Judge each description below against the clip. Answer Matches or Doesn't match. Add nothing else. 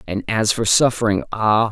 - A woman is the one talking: Doesn't match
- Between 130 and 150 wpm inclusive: Matches